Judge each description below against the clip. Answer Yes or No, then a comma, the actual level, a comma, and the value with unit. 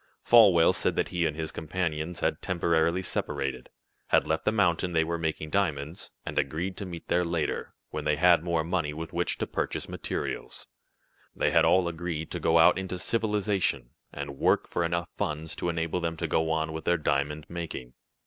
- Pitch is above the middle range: No, very low, 85 Hz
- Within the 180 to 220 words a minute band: Yes, average, 190 wpm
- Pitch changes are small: Yes, narrow, 2.3 semitones